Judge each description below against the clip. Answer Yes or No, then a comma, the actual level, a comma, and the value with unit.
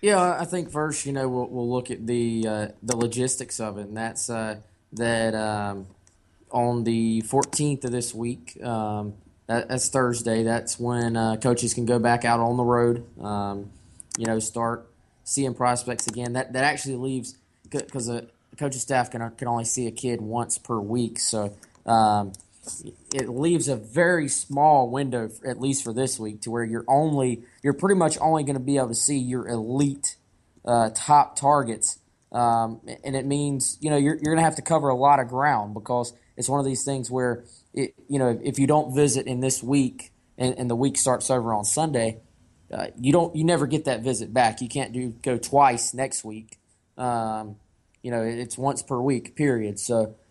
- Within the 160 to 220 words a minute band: Yes, average, 195 wpm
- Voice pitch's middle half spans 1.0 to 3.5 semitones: Yes, average, 3.1 semitones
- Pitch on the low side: Yes, low, 120 Hz